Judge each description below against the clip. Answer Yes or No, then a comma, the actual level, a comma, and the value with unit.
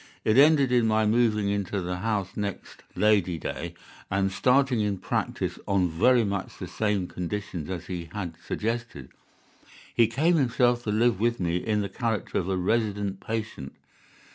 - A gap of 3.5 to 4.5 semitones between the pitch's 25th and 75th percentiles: Yes, average, 3.9 semitones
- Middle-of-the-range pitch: No, low, 105 Hz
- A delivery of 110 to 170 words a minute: Yes, average, 165 wpm